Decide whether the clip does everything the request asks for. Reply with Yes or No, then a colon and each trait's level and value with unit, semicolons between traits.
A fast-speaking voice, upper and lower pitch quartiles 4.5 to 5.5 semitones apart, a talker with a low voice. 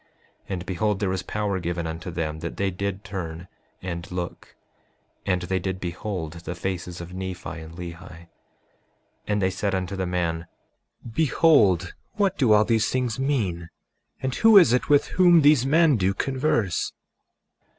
No: average, 160 wpm; average, 4.8 semitones; very low, 95 Hz